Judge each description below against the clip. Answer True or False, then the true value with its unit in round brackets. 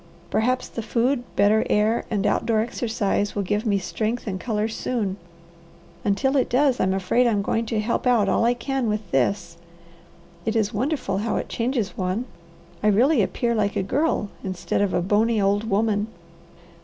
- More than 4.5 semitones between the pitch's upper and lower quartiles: False (3.0 semitones)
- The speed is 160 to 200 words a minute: True (175 wpm)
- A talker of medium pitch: False (215 Hz)